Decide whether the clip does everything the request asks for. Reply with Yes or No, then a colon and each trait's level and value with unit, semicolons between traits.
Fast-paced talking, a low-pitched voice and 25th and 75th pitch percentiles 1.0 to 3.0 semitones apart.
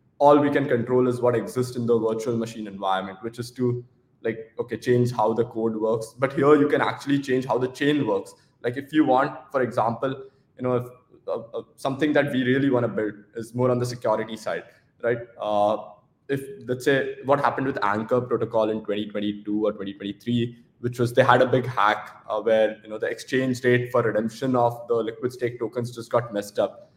Yes: fast, 210 wpm; low, 120 Hz; average, 2.7 semitones